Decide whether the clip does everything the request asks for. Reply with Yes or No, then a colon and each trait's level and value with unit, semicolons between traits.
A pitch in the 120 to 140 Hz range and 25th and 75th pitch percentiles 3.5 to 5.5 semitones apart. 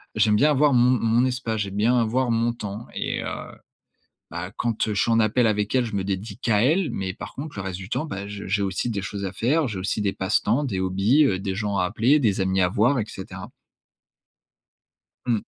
No: low, 110 Hz; average, 3.8 semitones